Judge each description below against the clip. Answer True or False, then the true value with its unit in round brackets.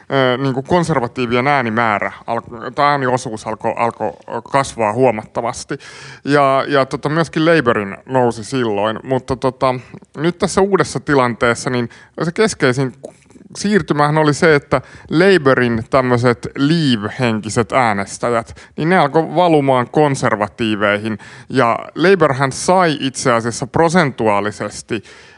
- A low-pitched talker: True (130 Hz)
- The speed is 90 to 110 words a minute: True (105 wpm)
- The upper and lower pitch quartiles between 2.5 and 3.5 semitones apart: False (4.4 semitones)